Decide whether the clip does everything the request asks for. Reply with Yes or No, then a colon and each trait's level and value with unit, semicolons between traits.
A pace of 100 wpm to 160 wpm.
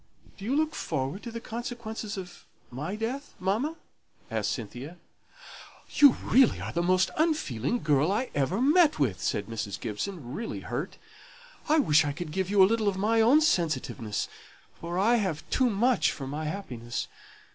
No: average, 170 wpm